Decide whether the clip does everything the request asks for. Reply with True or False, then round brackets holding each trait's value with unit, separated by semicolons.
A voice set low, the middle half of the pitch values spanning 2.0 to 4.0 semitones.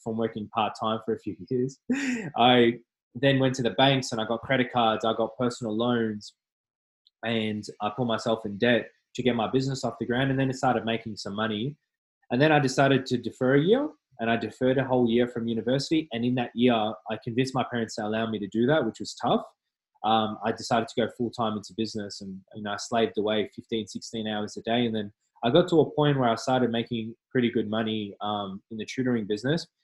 True (115 Hz; 2.8 semitones)